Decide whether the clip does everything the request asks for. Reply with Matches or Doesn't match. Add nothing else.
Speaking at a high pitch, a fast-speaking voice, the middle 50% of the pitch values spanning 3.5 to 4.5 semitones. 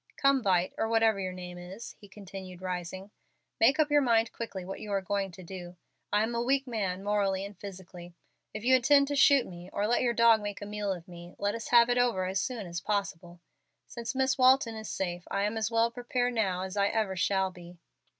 Matches